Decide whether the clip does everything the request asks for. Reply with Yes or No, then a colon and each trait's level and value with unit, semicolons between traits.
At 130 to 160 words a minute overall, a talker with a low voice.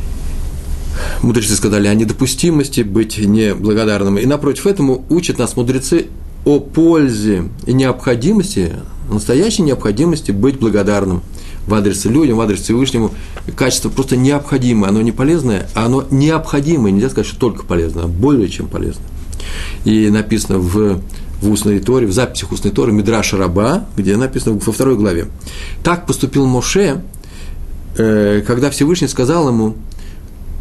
Yes: average, 135 wpm; low, 110 Hz